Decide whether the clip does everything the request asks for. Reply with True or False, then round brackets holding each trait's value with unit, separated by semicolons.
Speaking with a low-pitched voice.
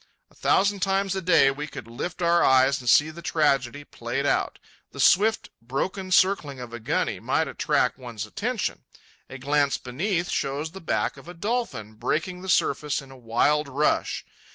False (150 Hz)